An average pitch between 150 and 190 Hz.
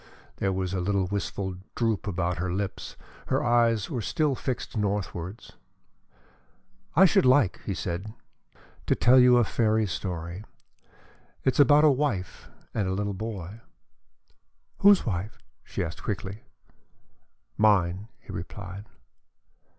No: low, 100 Hz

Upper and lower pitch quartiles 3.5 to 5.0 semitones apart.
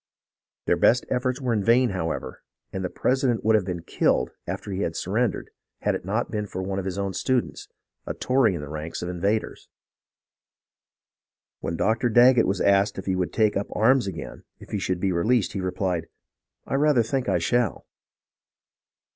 Yes: average, 4.6 semitones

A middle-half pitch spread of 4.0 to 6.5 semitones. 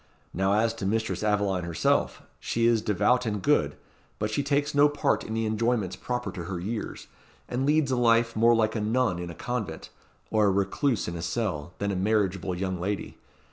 No: average, 3.6 semitones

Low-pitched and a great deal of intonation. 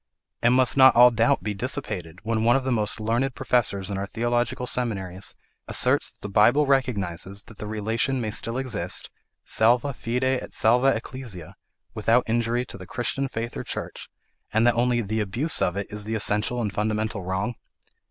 No: low, 115 Hz; average, 3.0 semitones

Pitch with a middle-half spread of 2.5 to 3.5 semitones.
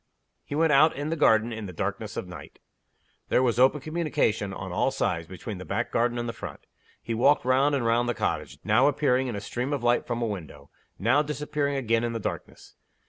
No: average, 4.3 semitones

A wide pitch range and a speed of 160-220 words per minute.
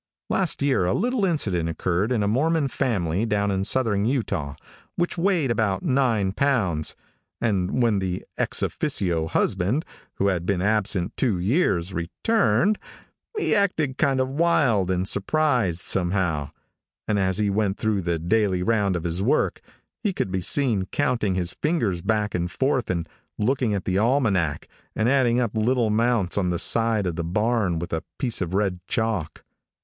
Yes: wide, 5.8 semitones; average, 165 wpm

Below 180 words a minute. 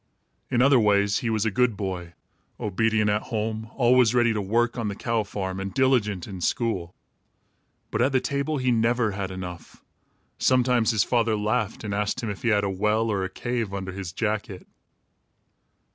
No: average, 185 wpm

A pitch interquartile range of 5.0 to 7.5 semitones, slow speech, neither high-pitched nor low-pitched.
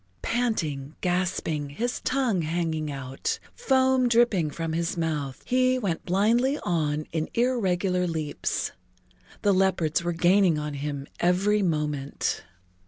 Yes: wide, 5.5 semitones; slow, 125 wpm; medium, 175 Hz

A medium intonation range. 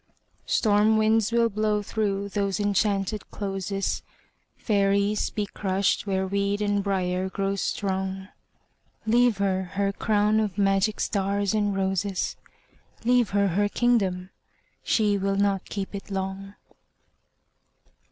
No: narrow, 1.3 semitones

